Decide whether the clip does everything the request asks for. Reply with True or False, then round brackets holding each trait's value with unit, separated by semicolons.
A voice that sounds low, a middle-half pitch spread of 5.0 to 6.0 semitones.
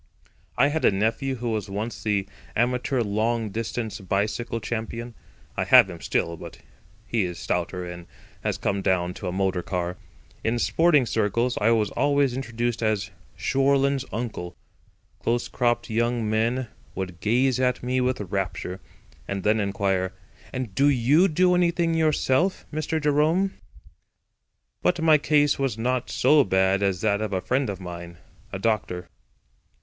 True (115 Hz; 5.3 semitones)